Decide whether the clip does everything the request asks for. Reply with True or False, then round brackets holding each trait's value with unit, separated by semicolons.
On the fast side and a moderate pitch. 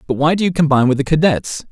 True (280 wpm; 150 Hz)